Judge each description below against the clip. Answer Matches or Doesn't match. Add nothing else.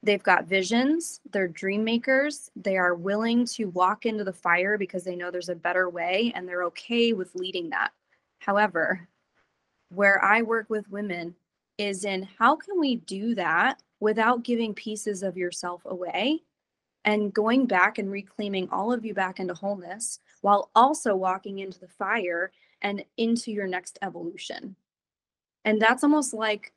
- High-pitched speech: Matches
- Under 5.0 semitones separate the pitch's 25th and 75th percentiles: Matches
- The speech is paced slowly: Doesn't match